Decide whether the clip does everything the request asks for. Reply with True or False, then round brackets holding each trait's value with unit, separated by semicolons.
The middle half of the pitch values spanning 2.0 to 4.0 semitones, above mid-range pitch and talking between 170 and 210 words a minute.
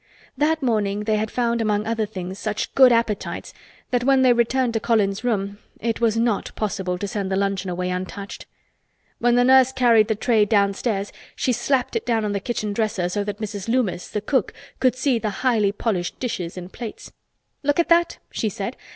True (3.5 semitones; 220 Hz; 195 wpm)